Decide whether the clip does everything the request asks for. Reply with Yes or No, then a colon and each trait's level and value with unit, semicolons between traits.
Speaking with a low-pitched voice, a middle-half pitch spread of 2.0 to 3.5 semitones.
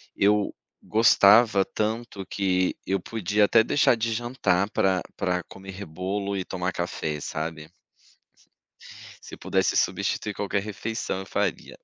Yes: low, 100 Hz; average, 2.7 semitones